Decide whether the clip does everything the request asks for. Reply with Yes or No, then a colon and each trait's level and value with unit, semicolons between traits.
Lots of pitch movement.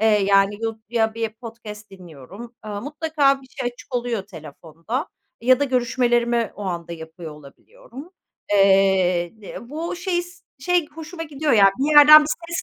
Yes: wide, 7.0 semitones